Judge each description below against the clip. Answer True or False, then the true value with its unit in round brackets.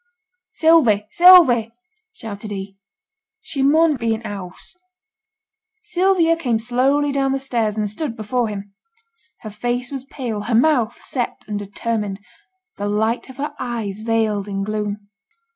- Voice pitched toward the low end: False (230 Hz)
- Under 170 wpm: True (145 wpm)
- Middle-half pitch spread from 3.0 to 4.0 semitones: False (4.5 semitones)